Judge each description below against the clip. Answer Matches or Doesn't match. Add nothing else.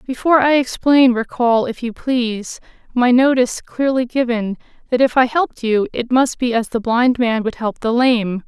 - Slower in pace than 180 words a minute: Doesn't match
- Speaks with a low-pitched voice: Doesn't match